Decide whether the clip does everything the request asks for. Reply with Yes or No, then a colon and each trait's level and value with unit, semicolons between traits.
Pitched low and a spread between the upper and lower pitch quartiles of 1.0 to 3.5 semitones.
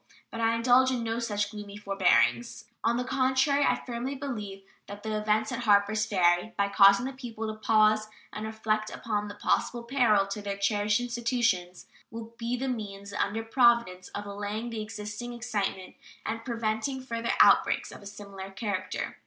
No: high, 215 Hz; average, 2.7 semitones